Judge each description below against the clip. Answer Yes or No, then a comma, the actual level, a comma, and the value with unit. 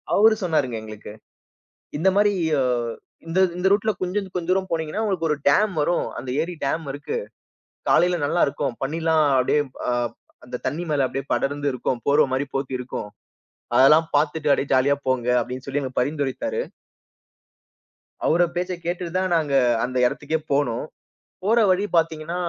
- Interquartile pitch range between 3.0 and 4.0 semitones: No, average, 4.6 semitones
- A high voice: No, medium, 155 Hz